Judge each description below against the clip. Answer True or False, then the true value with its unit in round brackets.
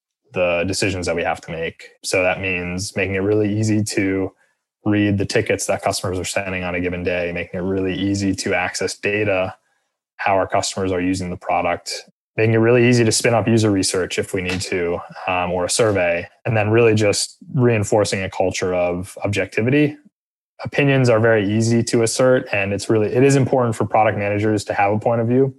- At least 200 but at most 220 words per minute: True (205 wpm)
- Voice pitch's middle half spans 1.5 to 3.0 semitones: False (3.6 semitones)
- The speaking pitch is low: True (100 Hz)